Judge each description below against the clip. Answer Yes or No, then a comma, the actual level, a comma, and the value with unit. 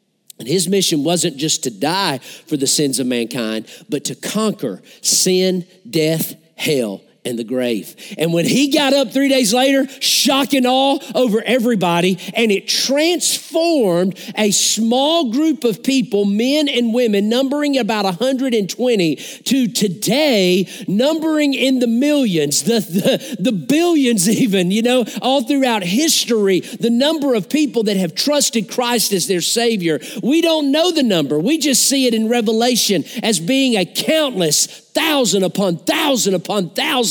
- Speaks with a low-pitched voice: No, high, 230 Hz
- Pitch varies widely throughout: Yes, wide, 6.2 semitones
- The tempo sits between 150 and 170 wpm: Yes, average, 155 wpm